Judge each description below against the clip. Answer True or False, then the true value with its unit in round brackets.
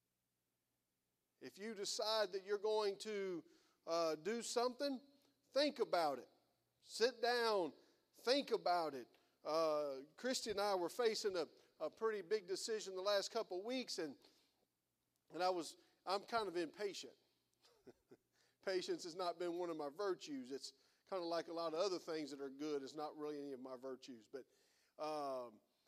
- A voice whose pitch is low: False (195 Hz)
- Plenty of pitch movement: True (8.3 semitones)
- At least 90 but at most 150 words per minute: False (165 wpm)